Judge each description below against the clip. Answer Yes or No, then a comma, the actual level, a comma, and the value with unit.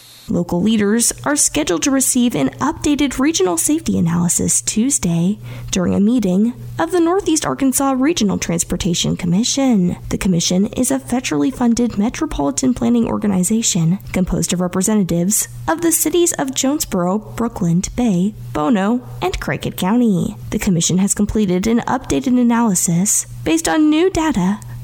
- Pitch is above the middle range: Yes, high, 210 Hz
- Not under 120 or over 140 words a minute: Yes, slow, 135 wpm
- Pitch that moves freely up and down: Yes, wide, 6.5 semitones